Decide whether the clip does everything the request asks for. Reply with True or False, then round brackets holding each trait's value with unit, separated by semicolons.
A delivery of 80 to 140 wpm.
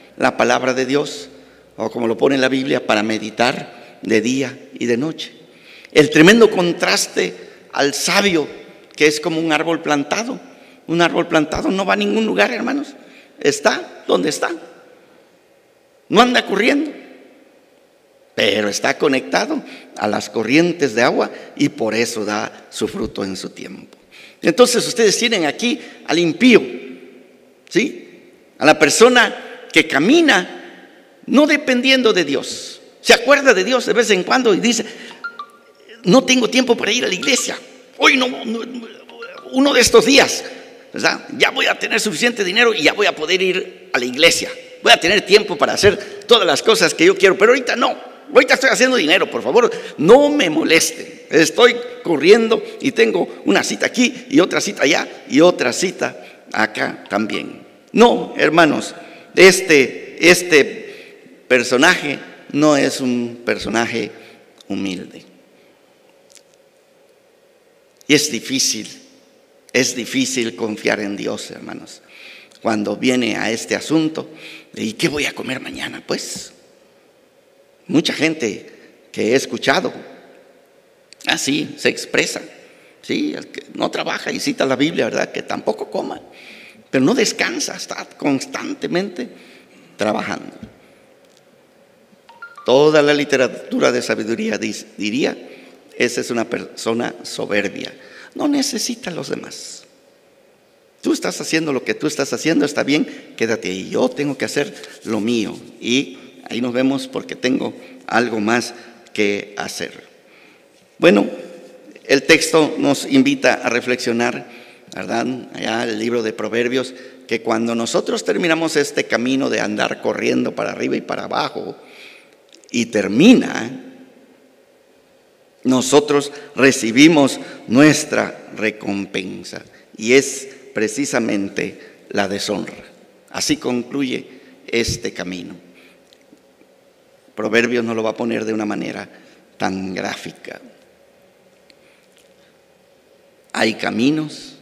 True (130 wpm)